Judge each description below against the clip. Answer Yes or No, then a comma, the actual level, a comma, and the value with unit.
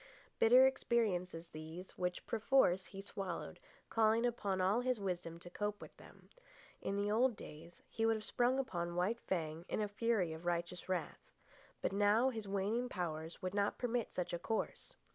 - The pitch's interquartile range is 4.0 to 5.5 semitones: Yes, average, 4.4 semitones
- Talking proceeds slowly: No, average, 175 wpm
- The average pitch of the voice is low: No, high, 200 Hz